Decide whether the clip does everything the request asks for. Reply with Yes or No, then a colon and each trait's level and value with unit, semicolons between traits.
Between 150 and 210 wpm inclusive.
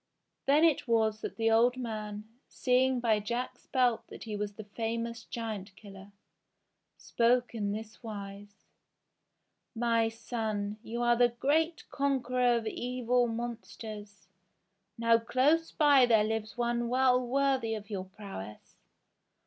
No: slow, 135 wpm